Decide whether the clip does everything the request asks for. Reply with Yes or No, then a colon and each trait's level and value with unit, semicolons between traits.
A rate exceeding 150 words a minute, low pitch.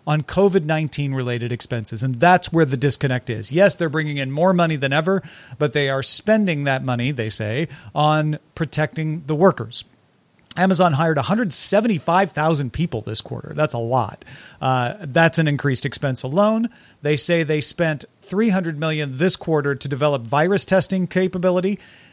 No: average, 185 wpm; medium, 155 Hz